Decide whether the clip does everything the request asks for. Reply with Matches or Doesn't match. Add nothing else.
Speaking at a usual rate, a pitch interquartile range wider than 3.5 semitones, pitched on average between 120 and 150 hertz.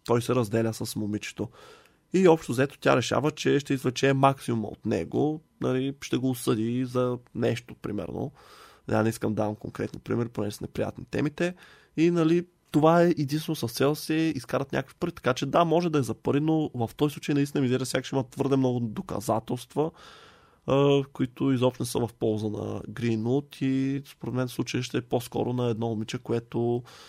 Doesn't match